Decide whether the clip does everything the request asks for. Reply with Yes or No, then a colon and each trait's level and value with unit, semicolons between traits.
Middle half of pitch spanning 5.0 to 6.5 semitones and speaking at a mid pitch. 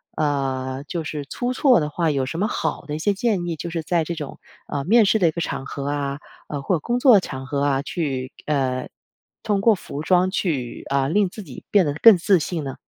Yes: average, 5.3 semitones; medium, 155 Hz